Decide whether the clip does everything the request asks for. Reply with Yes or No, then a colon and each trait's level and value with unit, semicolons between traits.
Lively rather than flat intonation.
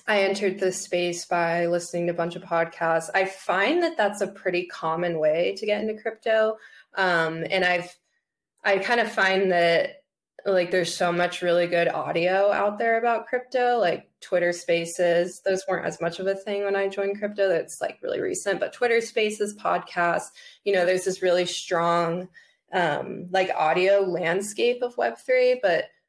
No: average, 3.6 semitones